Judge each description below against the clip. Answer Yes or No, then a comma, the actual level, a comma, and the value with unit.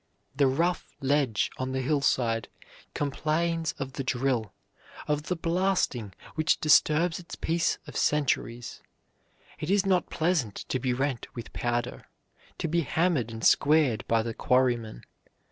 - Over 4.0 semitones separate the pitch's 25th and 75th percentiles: Yes, average, 5.1 semitones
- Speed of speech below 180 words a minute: Yes, average, 140 wpm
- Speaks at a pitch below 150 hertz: Yes, medium, 140 Hz